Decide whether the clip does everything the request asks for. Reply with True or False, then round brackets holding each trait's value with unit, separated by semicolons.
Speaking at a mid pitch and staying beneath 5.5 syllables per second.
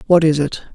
False (155 Hz; 6.3 syllables/s)